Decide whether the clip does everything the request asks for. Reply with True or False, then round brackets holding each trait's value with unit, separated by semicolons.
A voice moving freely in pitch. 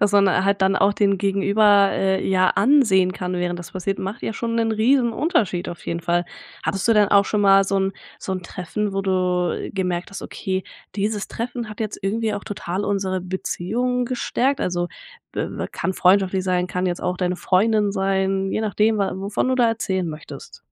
False (2.5 semitones)